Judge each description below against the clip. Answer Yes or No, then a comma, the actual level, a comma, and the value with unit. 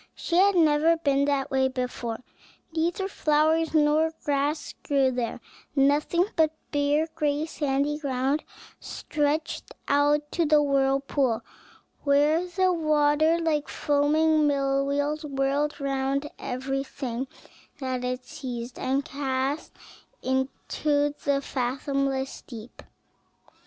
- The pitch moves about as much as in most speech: No, narrow, 2.2 semitones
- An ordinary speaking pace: No, slow, 110 wpm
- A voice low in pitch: No, very high, 285 Hz